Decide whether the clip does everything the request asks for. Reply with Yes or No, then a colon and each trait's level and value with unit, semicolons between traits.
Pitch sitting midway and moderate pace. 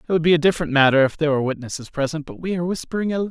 No: medium, 155 Hz; fast, 290 wpm